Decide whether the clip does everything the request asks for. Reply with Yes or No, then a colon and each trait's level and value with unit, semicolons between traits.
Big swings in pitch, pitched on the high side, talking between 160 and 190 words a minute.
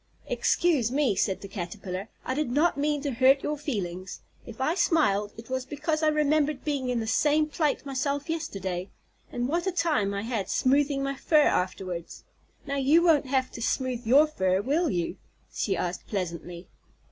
Yes: wide, 7.0 semitones; very high, 265 Hz; average, 180 wpm